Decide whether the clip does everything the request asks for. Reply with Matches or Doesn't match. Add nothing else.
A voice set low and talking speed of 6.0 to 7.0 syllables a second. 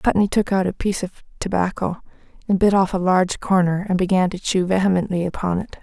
Doesn't match